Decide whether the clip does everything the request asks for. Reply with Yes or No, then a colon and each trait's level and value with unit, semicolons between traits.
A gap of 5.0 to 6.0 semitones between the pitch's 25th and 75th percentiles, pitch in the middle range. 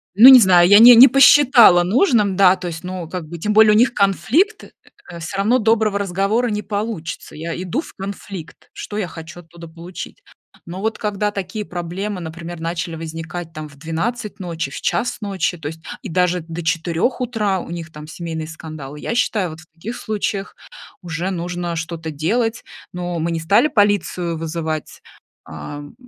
No: average, 4.3 semitones; medium, 180 Hz